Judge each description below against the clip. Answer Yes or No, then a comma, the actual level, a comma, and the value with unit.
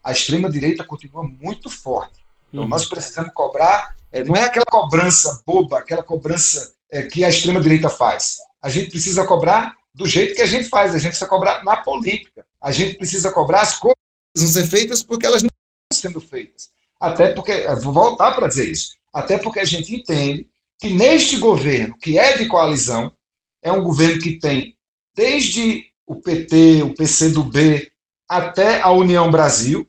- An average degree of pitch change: No, wide, 5.7 semitones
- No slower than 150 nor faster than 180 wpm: Yes, average, 175 wpm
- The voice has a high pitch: No, medium, 175 Hz